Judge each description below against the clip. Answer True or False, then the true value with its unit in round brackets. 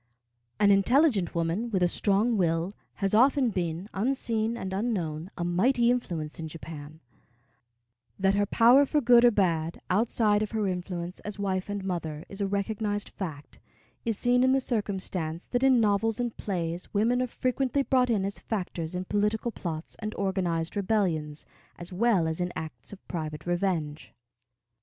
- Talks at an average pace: True (165 wpm)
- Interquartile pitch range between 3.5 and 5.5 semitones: True (4.8 semitones)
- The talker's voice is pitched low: False (195 Hz)